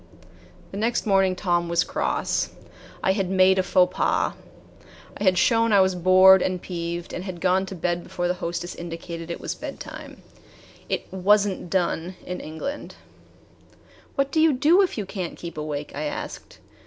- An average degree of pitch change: No, narrow, 2.1 semitones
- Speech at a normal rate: Yes, average, 175 wpm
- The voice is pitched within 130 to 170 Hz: No, medium, 185 Hz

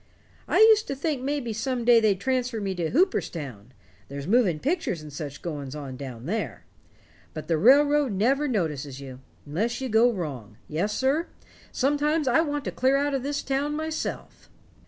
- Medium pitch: No, high, 235 Hz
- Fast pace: No, average, 180 wpm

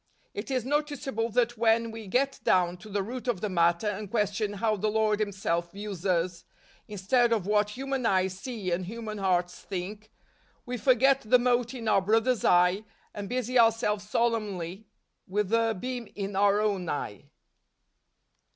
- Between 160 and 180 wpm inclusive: Yes, average, 165 wpm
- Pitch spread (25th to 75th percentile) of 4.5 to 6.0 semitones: No, average, 3.4 semitones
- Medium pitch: No, high, 210 Hz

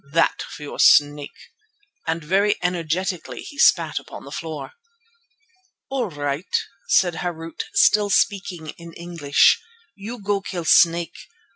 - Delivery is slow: Yes, slow, 125 wpm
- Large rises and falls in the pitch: No, average, 3.6 semitones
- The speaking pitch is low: No, medium, 170 Hz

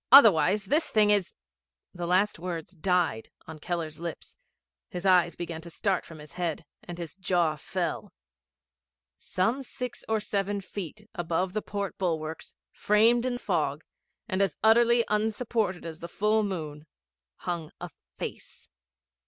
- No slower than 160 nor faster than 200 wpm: No, average, 145 wpm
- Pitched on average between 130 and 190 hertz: Yes, medium, 185 Hz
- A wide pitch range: No, average, 4.0 semitones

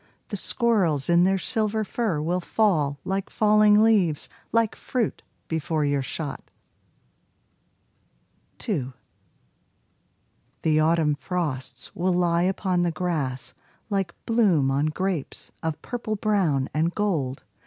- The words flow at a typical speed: No, slow, 115 wpm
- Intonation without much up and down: No, wide, 5.6 semitones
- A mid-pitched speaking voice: Yes, medium, 175 Hz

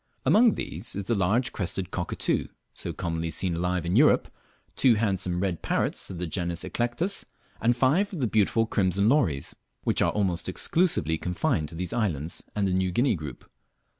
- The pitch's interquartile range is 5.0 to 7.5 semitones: Yes, wide, 5.4 semitones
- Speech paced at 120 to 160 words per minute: No, average, 180 wpm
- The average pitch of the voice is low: Yes, very low, 95 Hz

